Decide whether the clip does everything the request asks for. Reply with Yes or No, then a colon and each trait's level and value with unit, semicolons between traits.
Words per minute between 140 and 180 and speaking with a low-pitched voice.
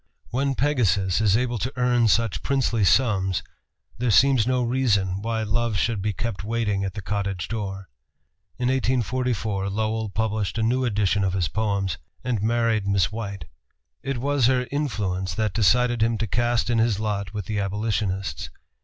Yes: average, 165 wpm; low, 110 Hz